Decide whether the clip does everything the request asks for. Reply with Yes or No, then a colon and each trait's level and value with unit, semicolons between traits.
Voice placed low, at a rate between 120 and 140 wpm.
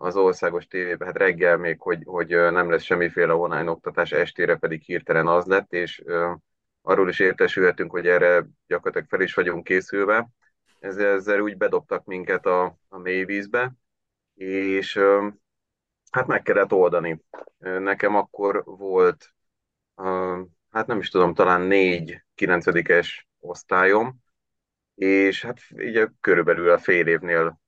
Yes: low, 125 Hz; average, 130 wpm